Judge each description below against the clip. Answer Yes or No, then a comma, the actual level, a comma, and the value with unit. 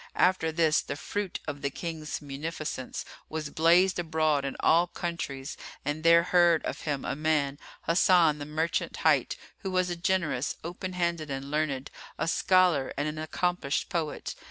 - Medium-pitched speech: Yes, medium, 160 Hz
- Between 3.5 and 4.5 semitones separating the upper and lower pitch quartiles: No, average, 3.0 semitones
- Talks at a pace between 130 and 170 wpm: Yes, average, 160 wpm